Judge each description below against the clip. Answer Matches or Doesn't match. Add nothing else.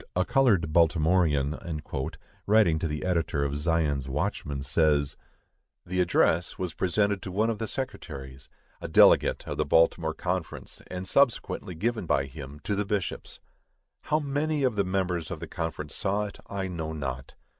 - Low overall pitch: Matches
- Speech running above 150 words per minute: Matches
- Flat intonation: Doesn't match